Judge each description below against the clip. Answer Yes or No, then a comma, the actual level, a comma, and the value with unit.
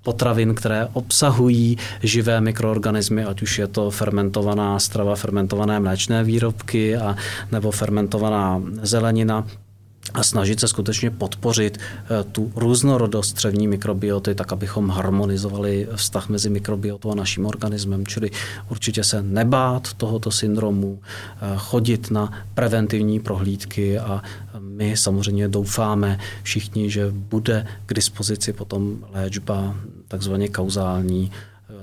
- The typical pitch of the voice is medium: No, low, 105 Hz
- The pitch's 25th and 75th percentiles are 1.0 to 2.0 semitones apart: Yes, narrow, 1.5 semitones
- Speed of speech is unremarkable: No, slow, 110 wpm